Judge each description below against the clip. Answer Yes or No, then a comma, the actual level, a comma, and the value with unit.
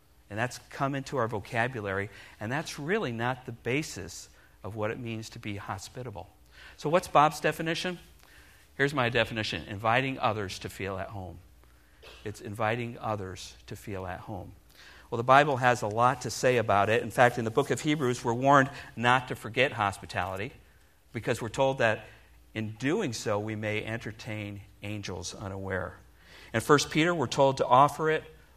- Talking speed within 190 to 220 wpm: No, average, 170 wpm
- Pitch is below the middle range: Yes, low, 115 Hz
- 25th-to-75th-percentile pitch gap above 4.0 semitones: Yes, average, 4.4 semitones